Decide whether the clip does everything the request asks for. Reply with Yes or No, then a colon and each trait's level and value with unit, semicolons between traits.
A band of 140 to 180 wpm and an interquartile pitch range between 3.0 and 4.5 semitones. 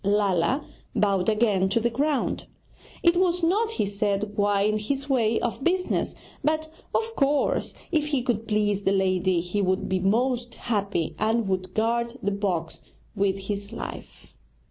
No: average, 160 wpm; average, 5.2 semitones